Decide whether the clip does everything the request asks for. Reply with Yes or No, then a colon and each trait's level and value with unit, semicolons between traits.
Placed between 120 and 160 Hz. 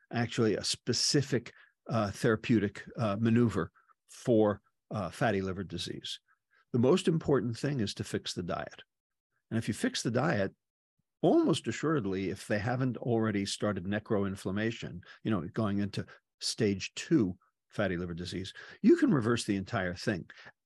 No: low, 110 Hz